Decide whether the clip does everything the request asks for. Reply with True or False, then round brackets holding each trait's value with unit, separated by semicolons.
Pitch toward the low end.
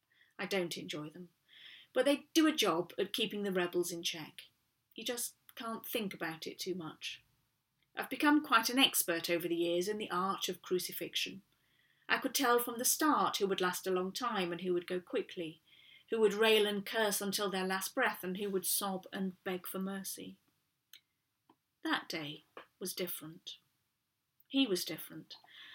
False (190 Hz)